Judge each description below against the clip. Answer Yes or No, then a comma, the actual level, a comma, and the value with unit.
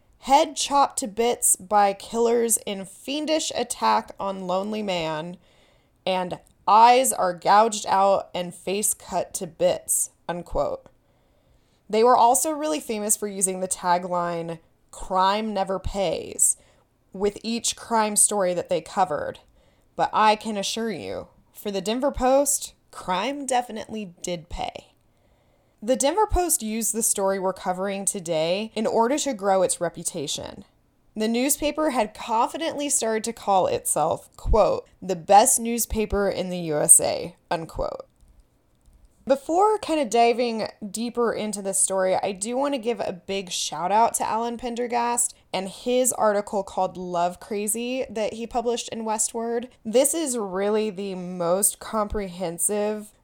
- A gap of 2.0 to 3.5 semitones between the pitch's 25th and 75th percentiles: No, average, 4.3 semitones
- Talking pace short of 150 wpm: Yes, average, 140 wpm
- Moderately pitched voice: No, high, 215 Hz